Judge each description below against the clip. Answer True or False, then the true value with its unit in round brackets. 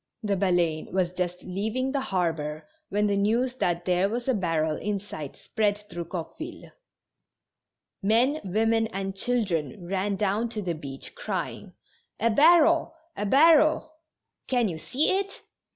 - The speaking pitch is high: True (205 Hz)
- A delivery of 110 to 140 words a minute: False (155 wpm)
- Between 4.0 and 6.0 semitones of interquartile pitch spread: True (5.6 semitones)